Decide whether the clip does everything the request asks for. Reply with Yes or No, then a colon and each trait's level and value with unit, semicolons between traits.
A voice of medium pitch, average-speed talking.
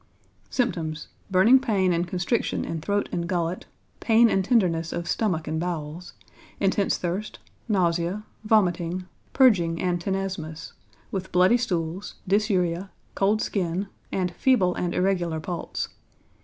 No: medium, 180 Hz; slow, 125 wpm